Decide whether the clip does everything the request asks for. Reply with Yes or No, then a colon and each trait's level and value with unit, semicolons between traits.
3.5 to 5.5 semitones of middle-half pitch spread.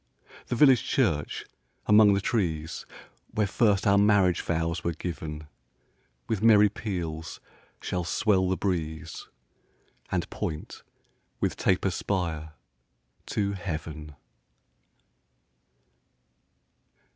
Yes: average, 4.4 semitones